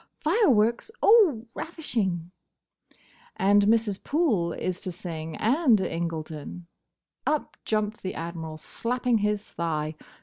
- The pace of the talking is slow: Yes, slow, 105 wpm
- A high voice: Yes, high, 205 Hz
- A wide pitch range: Yes, wide, 6.1 semitones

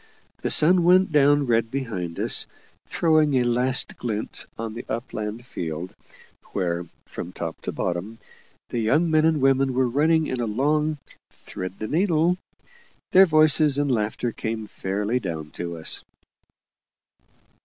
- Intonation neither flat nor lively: No, wide, 6.4 semitones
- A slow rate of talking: No, average, 145 wpm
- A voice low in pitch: Yes, low, 125 Hz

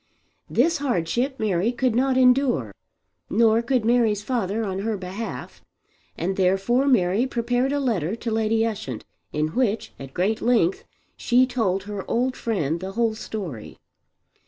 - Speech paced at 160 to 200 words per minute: No, average, 145 wpm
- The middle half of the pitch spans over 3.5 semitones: Yes, average, 4.5 semitones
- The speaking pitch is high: Yes, high, 220 Hz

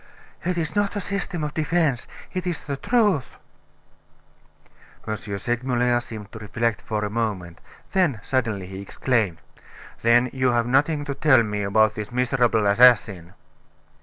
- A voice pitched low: Yes, low, 120 Hz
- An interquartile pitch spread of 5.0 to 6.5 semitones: Yes, wide, 5.4 semitones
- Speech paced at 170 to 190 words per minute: No, average, 145 wpm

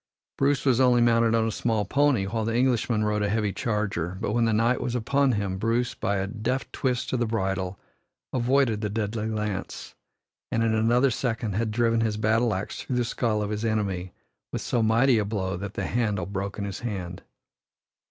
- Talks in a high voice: No, low, 110 Hz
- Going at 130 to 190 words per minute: No, average, 200 wpm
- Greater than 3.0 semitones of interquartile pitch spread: No, narrow, 2.6 semitones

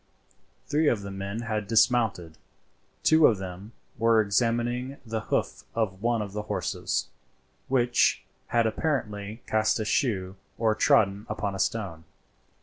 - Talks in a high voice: No, low, 110 Hz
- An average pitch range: Yes, average, 3.0 semitones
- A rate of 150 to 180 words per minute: No, average, 140 wpm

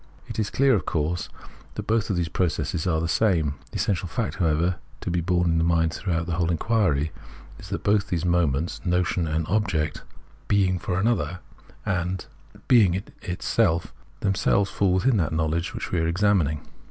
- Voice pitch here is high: No, very low, 90 Hz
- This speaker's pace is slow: No, average, 190 wpm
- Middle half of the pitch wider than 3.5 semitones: No, average, 3.2 semitones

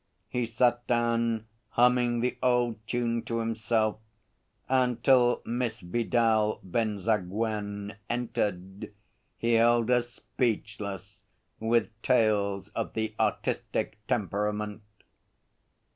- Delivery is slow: Yes, slow, 95 wpm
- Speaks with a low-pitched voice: Yes, low, 115 Hz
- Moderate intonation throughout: No, narrow, 2.2 semitones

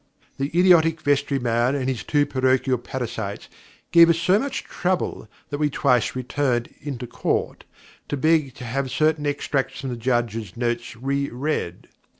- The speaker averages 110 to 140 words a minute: No, average, 155 wpm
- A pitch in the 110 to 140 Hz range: Yes, low, 135 Hz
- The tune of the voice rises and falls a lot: No, average, 3.4 semitones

